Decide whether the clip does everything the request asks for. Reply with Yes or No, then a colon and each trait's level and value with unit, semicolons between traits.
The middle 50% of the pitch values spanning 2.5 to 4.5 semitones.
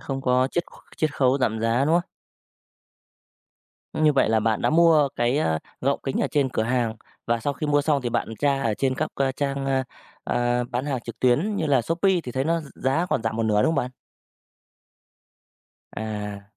Yes: average, 3.8 semitones